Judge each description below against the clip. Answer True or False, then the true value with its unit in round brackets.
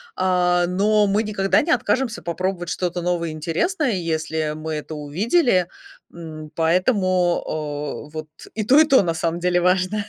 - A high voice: False (180 Hz)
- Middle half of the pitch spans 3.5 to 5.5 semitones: True (4.0 semitones)